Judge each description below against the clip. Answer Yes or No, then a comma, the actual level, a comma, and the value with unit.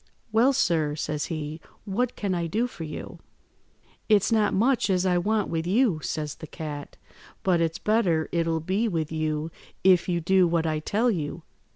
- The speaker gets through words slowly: No, average, 180 wpm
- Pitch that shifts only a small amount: No, average, 4.6 semitones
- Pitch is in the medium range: Yes, medium, 175 Hz